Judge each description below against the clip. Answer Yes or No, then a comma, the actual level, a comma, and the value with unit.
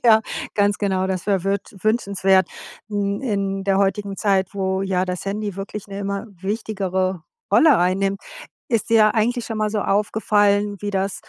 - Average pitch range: No, narrow, 1.5 semitones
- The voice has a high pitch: Yes, high, 200 Hz